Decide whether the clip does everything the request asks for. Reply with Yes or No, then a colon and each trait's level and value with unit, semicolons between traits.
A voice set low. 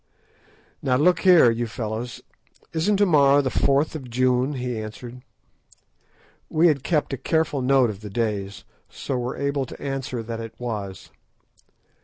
Yes: low, 125 Hz